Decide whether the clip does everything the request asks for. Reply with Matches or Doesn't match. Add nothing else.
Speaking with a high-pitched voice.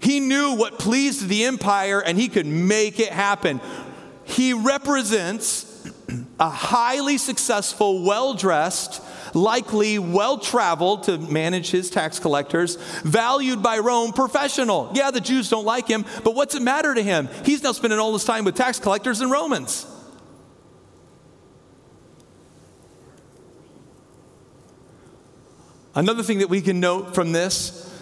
Matches